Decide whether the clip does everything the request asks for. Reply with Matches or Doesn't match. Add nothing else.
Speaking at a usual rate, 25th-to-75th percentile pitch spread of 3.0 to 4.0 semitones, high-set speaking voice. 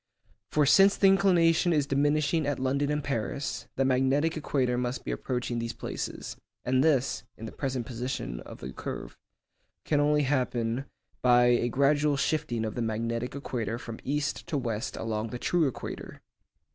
Doesn't match